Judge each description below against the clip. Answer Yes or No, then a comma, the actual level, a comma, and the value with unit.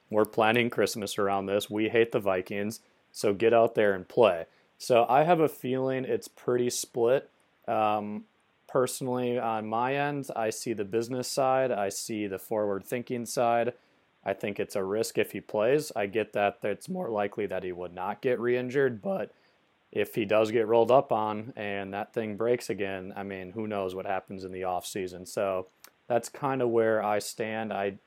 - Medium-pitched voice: No, low, 110 Hz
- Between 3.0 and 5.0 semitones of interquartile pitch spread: Yes, average, 3.5 semitones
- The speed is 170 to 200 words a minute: Yes, average, 190 wpm